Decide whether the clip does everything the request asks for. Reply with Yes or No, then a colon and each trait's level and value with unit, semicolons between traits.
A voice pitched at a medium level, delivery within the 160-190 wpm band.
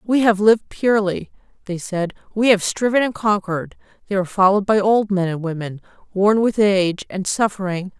No: high, 200 Hz; average, 180 wpm